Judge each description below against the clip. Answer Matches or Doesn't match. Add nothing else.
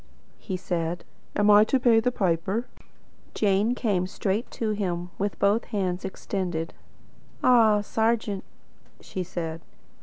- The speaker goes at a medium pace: Doesn't match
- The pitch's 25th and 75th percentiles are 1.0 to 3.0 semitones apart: Doesn't match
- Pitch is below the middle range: Doesn't match